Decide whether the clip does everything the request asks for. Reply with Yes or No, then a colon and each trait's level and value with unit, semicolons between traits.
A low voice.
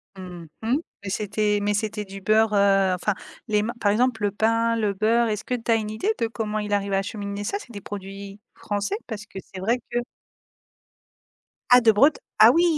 No: high, 210 Hz